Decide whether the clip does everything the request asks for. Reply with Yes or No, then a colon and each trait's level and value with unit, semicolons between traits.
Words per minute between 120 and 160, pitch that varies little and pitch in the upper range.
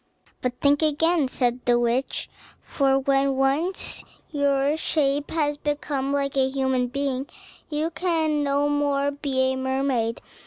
Yes: average, 140 wpm; narrow, 1.8 semitones; very high, 275 Hz